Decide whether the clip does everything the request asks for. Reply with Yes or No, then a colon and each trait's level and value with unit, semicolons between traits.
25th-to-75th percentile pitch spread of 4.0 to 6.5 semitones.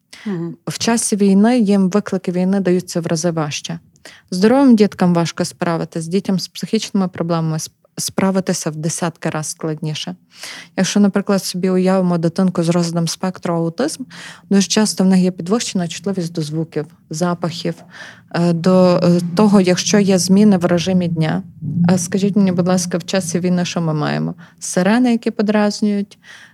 No: average, 2.7 semitones